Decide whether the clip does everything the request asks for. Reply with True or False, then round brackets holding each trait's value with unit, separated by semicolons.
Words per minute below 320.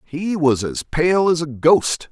True (200 wpm)